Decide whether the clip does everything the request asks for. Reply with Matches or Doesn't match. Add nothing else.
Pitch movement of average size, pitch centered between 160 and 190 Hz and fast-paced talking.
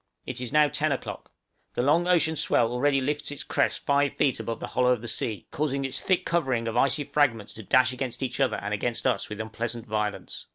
Doesn't match